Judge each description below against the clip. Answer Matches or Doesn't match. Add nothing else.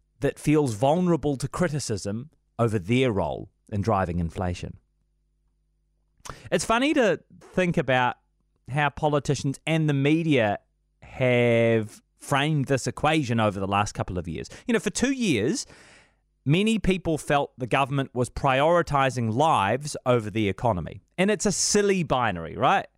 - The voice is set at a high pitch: Doesn't match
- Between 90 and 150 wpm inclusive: Matches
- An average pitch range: Doesn't match